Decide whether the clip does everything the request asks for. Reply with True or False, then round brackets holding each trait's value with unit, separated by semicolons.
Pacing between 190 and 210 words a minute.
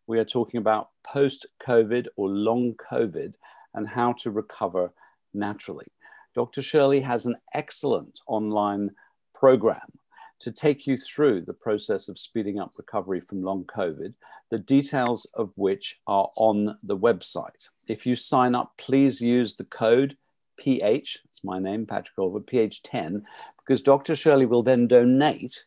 False (145 wpm)